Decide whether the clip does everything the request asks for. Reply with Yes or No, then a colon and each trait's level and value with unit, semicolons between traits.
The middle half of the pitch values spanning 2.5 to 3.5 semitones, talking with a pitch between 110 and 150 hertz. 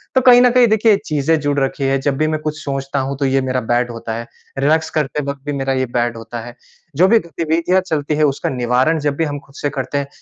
Yes: average, 2.9 semitones; medium, 140 Hz